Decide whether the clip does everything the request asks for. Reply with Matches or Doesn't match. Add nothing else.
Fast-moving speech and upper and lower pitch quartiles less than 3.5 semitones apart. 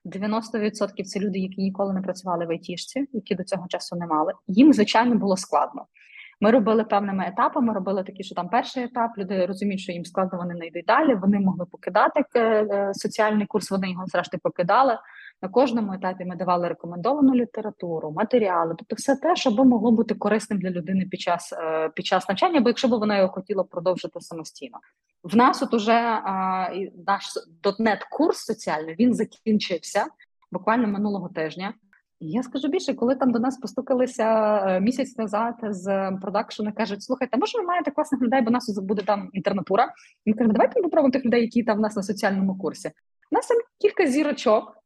Doesn't match